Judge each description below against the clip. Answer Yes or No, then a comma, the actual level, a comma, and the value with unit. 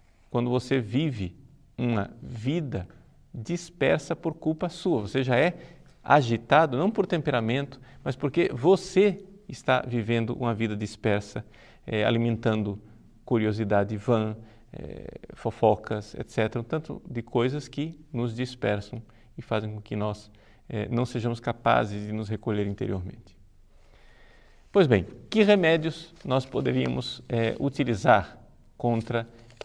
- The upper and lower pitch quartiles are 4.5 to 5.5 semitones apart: Yes, average, 5.0 semitones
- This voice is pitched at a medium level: No, low, 120 Hz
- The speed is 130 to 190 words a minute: No, slow, 120 wpm